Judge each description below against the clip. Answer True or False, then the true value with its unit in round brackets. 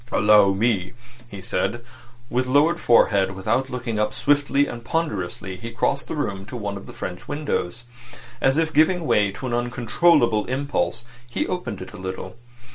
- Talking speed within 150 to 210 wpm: True (170 wpm)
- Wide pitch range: True (5.7 semitones)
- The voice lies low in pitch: True (120 Hz)